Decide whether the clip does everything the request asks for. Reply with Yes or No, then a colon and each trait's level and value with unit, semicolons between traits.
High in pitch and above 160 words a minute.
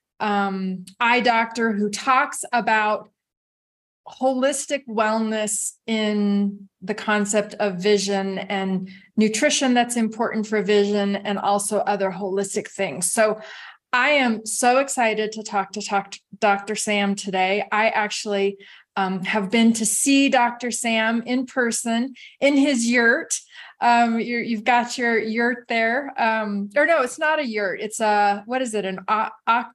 No: high, 215 Hz; average, 145 wpm